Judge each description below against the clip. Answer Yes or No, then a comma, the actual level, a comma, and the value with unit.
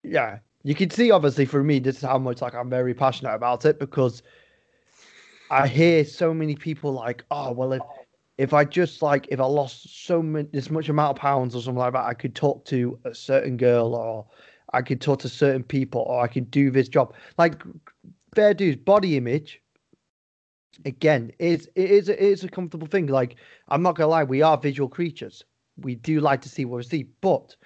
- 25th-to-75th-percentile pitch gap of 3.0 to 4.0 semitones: Yes, average, 3.7 semitones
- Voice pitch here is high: No, medium, 140 Hz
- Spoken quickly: Yes, fast, 210 wpm